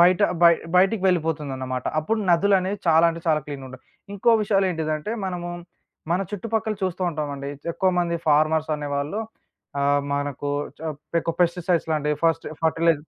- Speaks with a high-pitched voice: No, medium, 165 Hz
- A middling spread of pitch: Yes, average, 3.7 semitones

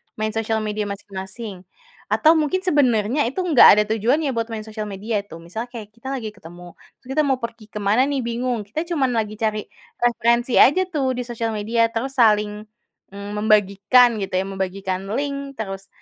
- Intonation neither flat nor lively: Yes, average, 3.5 semitones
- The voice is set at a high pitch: Yes, high, 225 Hz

